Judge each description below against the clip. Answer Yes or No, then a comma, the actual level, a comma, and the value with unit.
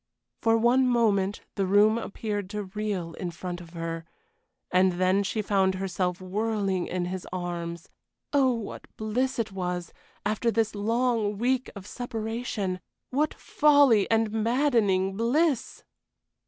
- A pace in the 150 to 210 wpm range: No, slow, 135 wpm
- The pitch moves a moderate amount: Yes, average, 3.7 semitones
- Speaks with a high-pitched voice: Yes, high, 205 Hz